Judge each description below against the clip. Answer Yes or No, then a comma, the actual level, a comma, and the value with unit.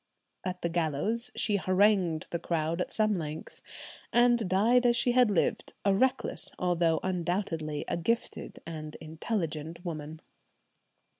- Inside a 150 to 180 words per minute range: No, slow, 135 wpm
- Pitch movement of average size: Yes, average, 4.9 semitones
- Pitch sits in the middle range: Yes, medium, 180 Hz